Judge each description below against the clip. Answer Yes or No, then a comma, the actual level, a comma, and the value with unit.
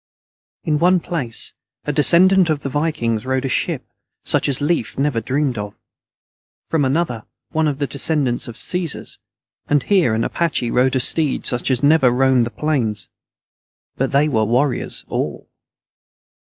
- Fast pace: No, average, 165 wpm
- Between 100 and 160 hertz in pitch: Yes, medium, 140 Hz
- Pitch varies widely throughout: No, average, 4.1 semitones